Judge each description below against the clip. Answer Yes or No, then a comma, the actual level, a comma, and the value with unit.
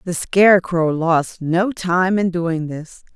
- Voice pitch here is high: No, medium, 175 Hz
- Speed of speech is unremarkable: Yes, average, 150 wpm